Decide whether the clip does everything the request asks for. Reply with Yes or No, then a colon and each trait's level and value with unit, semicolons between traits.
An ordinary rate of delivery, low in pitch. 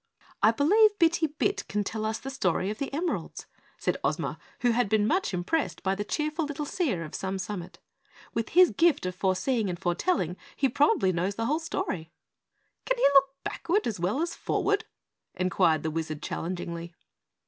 No: average, 180 wpm; high, 220 Hz